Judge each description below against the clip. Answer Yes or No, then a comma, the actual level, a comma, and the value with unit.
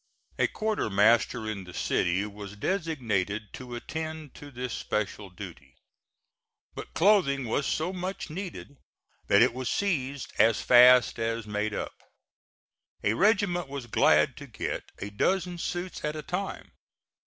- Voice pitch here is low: Yes, low, 125 Hz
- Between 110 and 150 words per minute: Yes, average, 140 wpm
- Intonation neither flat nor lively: No, wide, 8.1 semitones